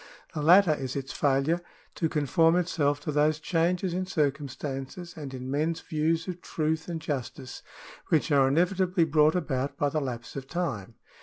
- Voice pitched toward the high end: No, medium, 155 Hz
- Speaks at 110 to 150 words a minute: No, average, 165 wpm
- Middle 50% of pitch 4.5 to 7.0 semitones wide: No, average, 3.3 semitones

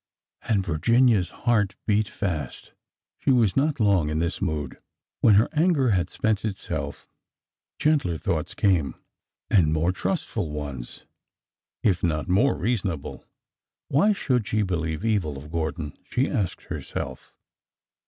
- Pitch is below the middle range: Yes, very low, 95 Hz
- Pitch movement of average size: No, wide, 6.3 semitones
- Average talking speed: No, slow, 130 wpm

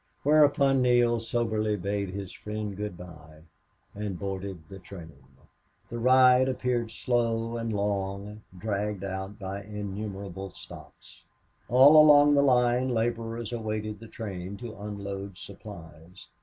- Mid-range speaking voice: No, low, 105 Hz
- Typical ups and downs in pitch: Yes, average, 3.4 semitones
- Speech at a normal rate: No, slow, 125 wpm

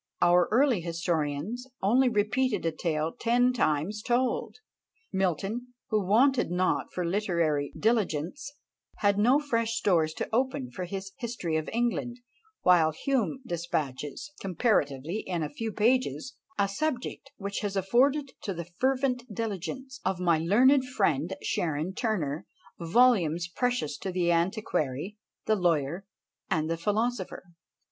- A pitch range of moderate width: No, wide, 6.3 semitones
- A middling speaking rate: No, slow, 130 wpm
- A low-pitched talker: No, high, 195 Hz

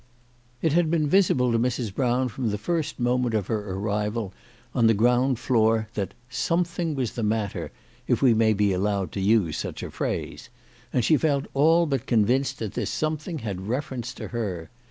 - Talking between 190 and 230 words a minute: Yes, average, 195 wpm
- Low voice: Yes, low, 120 Hz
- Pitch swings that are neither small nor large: Yes, average, 4.7 semitones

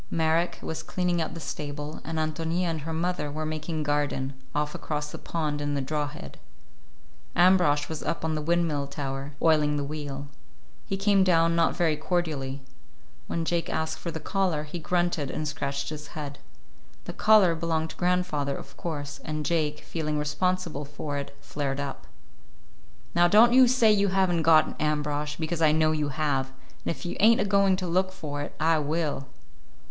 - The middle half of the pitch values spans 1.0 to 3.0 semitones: Yes, average, 2.7 semitones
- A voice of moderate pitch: Yes, medium, 155 Hz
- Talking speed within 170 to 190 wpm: Yes, average, 185 wpm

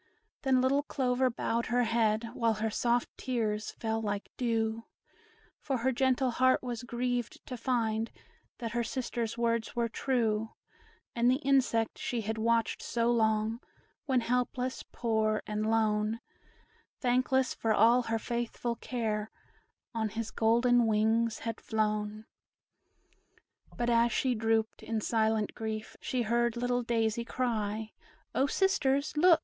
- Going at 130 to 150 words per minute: Yes, slow, 135 wpm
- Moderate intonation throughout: No, narrow, 2.0 semitones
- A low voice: No, high, 230 Hz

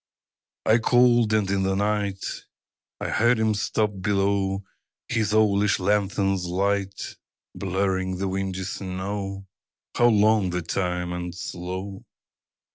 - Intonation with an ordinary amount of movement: No, narrow, 1.8 semitones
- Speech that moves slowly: Yes, slow, 120 wpm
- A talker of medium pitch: No, low, 100 Hz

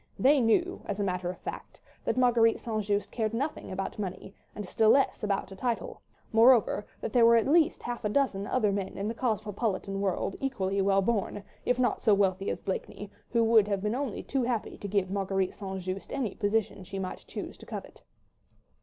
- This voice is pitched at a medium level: No, high, 210 Hz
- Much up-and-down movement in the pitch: No, average, 3.3 semitones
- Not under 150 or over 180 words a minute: No, average, 200 wpm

